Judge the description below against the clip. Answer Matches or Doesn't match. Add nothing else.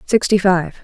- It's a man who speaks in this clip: Doesn't match